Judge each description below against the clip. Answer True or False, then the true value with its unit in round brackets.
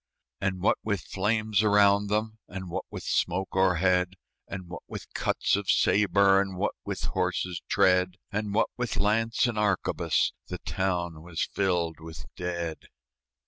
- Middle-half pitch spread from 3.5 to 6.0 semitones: False (2.5 semitones)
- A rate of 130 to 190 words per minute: True (150 wpm)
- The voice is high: False (95 Hz)